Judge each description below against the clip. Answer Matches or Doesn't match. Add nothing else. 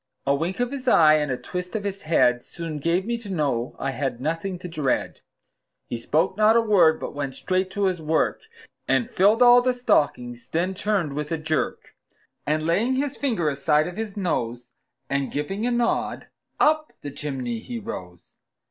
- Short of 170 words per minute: Doesn't match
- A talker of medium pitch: Matches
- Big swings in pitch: Matches